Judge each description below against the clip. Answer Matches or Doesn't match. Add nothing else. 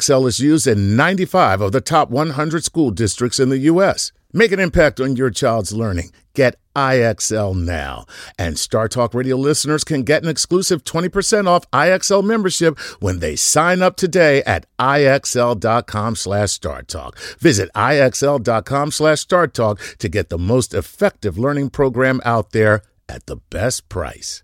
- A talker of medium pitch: Doesn't match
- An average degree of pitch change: Doesn't match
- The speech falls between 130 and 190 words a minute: Matches